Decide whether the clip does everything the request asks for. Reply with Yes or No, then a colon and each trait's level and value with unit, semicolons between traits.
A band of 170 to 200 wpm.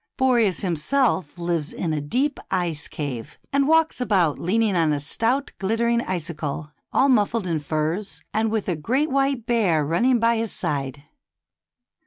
Yes: average, 175 wpm